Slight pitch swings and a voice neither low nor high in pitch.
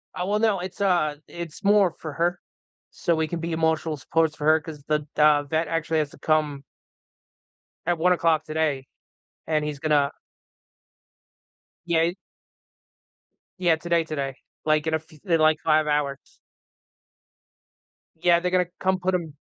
Yes: narrow, 2.2 semitones; medium, 160 Hz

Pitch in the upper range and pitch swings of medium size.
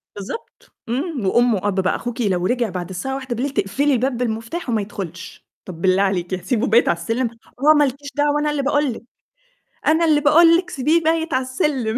No: very high, 250 Hz; wide, 6.5 semitones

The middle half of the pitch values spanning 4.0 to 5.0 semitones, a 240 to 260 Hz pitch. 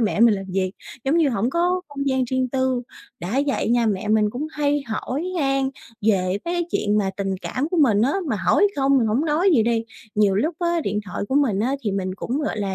No: wide, 5.6 semitones; high, 245 Hz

